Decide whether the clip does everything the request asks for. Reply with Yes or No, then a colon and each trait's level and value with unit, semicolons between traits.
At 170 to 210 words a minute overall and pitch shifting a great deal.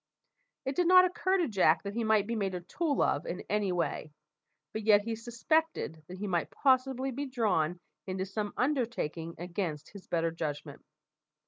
Yes: average, 180 wpm; wide, 6.8 semitones